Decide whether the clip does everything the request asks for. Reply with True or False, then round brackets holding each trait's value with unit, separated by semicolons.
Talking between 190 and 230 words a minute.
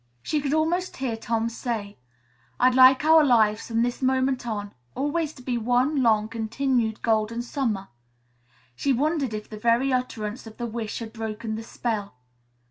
False (165 wpm)